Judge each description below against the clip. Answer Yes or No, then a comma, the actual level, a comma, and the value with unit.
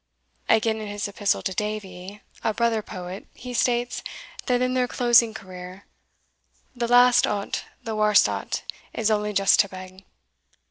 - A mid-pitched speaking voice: No, high, 215 Hz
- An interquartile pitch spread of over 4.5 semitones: No, average, 3.2 semitones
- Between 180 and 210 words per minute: No, average, 150 wpm